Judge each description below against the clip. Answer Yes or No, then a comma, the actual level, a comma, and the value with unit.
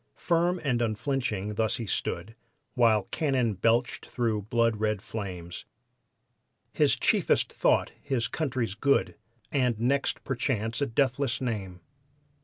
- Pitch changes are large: No, average, 3.9 semitones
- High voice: No, low, 115 Hz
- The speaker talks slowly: Yes, slow, 120 wpm